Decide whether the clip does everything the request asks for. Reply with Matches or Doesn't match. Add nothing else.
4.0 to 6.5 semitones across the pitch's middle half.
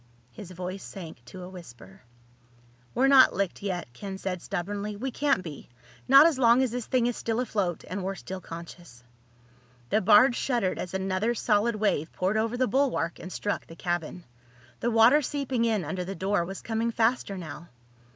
Matches